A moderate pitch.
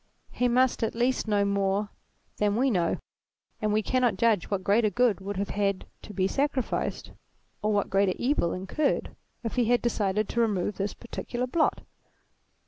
No: high, 210 Hz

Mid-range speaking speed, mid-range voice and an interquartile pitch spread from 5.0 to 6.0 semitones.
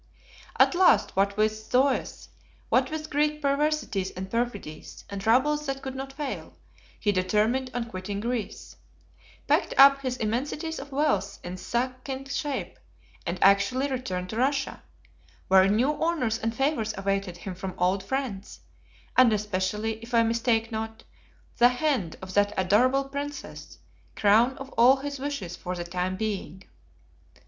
No: average, 145 wpm; high, 230 Hz; wide, 5.4 semitones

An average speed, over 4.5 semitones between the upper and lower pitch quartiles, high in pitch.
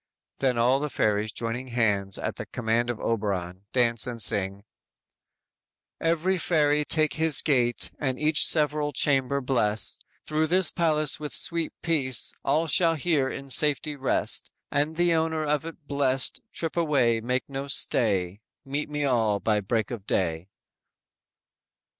No: average, 150 wpm; average, 5.0 semitones; low, 135 Hz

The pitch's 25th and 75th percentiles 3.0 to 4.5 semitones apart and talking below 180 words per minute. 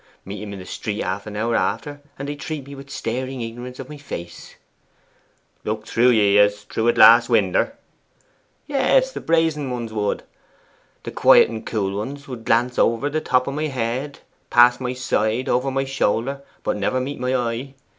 No: average, 4.0 semitones; average, 185 wpm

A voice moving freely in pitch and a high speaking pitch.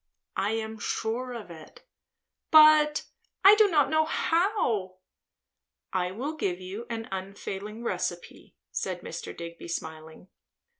Yes: wide, 8.3 semitones; high, 220 Hz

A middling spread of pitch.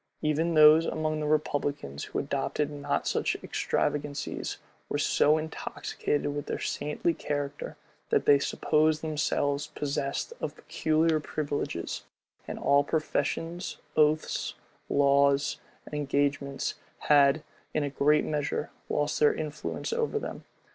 No: narrow, 1.4 semitones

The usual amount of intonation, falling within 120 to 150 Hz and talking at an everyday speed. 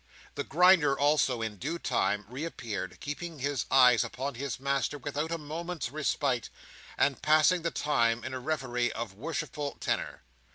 Yes: average, 3.9 semitones; medium, 140 Hz; average, 155 wpm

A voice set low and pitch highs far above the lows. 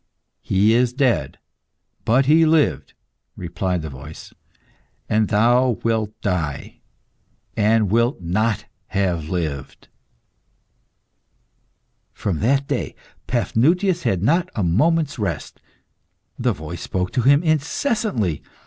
Yes: low, 110 Hz; wide, 7.1 semitones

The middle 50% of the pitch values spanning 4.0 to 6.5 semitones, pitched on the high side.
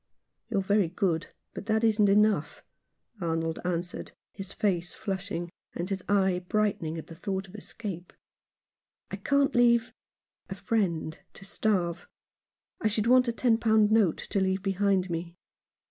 No: average, 3.6 semitones; high, 195 Hz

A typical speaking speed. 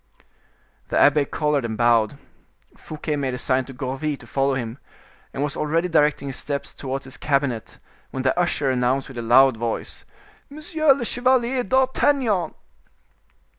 Yes: average, 155 wpm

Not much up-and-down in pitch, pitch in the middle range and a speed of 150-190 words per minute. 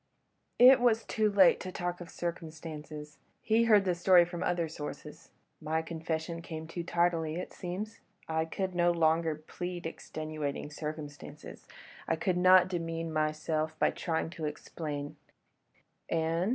No: narrow, 2.3 semitones; medium, 165 Hz; average, 140 wpm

